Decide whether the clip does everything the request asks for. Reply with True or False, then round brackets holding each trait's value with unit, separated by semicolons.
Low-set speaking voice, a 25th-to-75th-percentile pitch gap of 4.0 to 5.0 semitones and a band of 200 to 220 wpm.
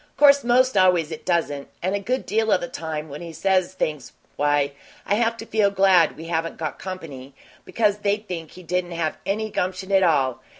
False (180 Hz; 4.3 semitones; 205 wpm)